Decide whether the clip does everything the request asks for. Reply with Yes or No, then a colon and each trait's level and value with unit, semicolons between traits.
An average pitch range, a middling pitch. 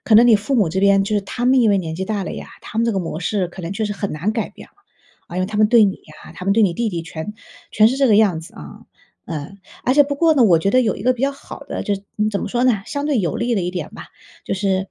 No: average, 4.2 semitones; high, 205 Hz